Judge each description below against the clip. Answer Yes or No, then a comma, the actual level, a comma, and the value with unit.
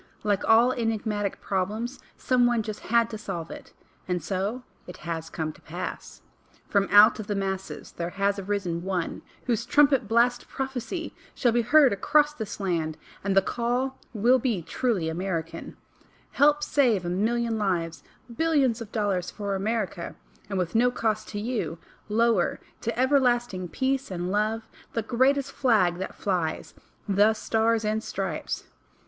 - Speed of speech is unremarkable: Yes, average, 155 wpm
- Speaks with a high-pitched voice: Yes, high, 215 Hz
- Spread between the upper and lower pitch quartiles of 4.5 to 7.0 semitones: No, average, 4.1 semitones